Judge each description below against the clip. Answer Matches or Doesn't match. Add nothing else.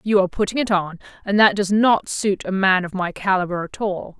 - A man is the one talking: Doesn't match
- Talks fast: Matches